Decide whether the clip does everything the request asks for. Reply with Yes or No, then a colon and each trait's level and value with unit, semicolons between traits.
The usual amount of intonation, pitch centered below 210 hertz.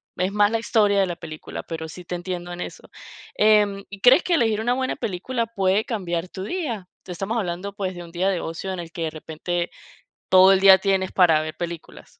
Yes: average, 3.2 semitones; high, 190 Hz